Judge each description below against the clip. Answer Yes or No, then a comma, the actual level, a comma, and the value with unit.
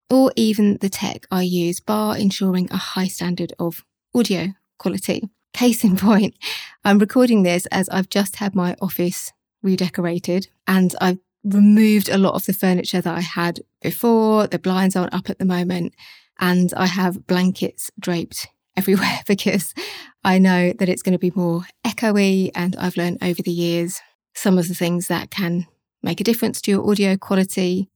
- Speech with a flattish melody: Yes, narrow, 2.2 semitones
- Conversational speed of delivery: Yes, average, 175 wpm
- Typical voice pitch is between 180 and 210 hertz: Yes, high, 190 Hz